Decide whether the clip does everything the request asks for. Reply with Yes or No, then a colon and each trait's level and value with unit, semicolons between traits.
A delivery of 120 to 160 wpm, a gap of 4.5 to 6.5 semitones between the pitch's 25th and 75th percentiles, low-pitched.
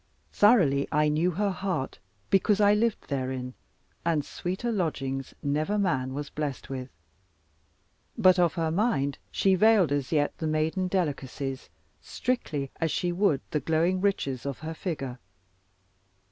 No: average, 140 wpm; average, 5.3 semitones; medium, 160 Hz